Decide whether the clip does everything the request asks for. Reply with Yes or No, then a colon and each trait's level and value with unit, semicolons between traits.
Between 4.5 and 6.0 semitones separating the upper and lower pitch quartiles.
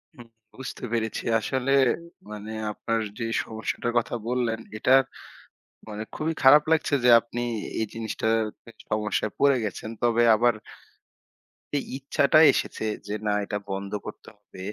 No: average, 2.9 semitones